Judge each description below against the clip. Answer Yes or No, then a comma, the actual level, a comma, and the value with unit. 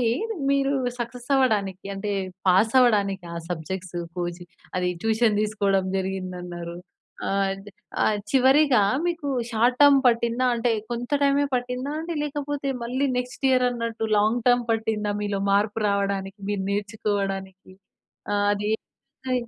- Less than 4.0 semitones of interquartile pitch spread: No, average, 4.3 semitones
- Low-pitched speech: No, high, 220 Hz